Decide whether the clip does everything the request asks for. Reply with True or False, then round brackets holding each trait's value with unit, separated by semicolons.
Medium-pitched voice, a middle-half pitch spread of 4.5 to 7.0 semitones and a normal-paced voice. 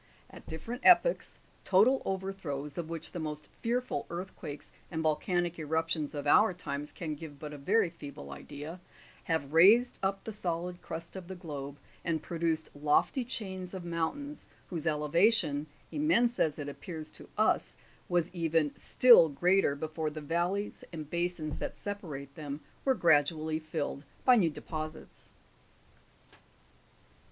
False (165 Hz; 3.9 semitones; 145 wpm)